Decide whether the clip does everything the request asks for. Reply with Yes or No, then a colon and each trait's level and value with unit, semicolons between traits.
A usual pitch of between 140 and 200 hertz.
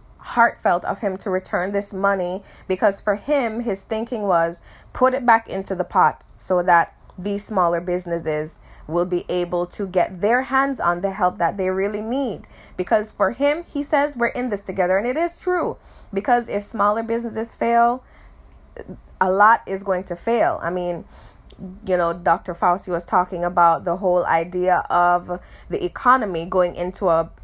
Yes: high, 190 Hz